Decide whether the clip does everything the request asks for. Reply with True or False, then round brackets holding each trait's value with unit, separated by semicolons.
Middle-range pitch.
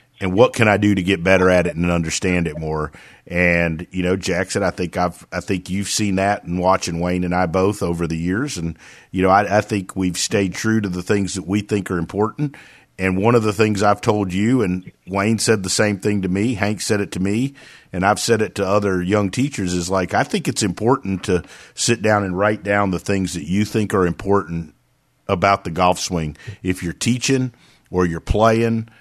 False (95 Hz)